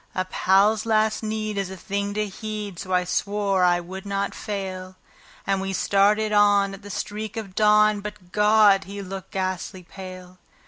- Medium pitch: No, high, 200 Hz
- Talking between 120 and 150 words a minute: No, average, 175 wpm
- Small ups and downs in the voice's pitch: Yes, narrow, 1.9 semitones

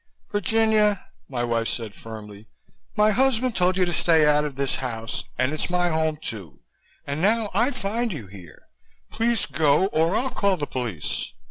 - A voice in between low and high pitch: Yes, medium, 160 Hz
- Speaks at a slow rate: No, average, 170 wpm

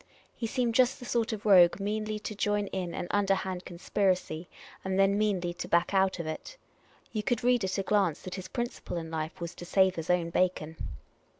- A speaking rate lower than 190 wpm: No, fast, 205 wpm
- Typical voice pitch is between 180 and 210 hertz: Yes, high, 190 Hz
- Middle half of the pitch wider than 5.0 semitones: No, average, 3.2 semitones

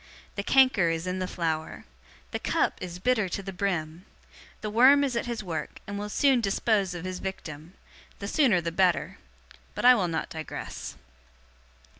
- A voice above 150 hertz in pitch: Yes, high, 190 Hz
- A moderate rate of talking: Yes, average, 175 wpm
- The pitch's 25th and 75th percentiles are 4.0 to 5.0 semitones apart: Yes, average, 4.7 semitones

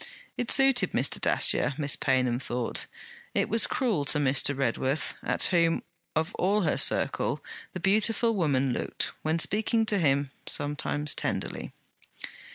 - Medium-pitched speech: Yes, medium, 155 Hz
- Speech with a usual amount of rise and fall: No, wide, 7.1 semitones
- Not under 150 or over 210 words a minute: No, average, 140 wpm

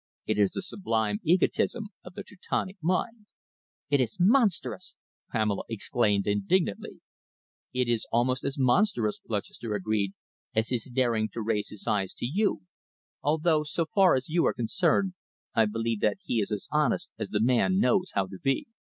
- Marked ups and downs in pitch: Yes, wide, 8.7 semitones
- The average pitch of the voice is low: Yes, low, 125 Hz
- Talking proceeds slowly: No, average, 165 wpm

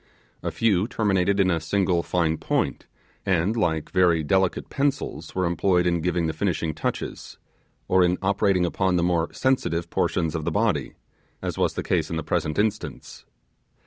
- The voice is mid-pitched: No, very low, 90 Hz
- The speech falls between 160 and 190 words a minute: Yes, average, 170 wpm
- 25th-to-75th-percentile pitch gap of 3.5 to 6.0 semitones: No, average, 2.8 semitones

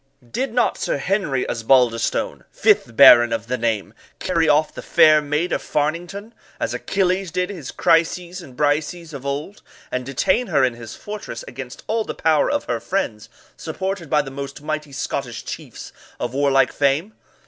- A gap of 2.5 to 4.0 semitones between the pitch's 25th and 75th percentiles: No, wide, 5.5 semitones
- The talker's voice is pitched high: No, medium, 150 Hz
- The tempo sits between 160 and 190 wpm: Yes, average, 170 wpm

